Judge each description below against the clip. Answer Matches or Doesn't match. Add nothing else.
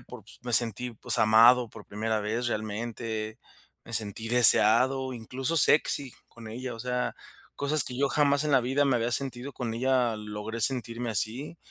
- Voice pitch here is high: Doesn't match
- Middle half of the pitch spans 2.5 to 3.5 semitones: Matches